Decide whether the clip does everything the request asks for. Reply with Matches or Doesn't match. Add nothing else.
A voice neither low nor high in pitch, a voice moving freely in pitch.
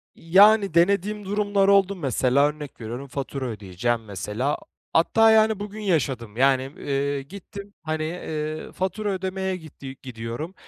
Matches